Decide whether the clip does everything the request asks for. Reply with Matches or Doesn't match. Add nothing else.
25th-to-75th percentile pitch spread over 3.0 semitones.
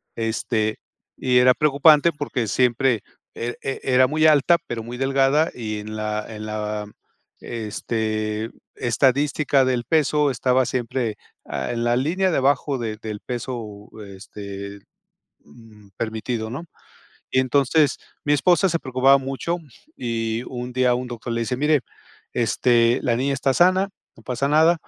Matches